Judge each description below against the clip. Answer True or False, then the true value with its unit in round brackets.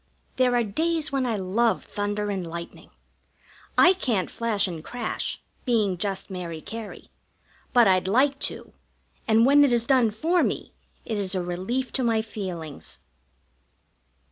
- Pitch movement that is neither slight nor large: True (4.7 semitones)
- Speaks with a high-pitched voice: True (220 Hz)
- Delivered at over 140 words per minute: True (150 wpm)